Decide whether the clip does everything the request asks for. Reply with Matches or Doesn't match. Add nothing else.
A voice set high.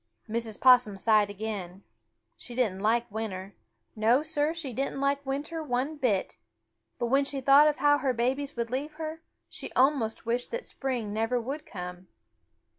Matches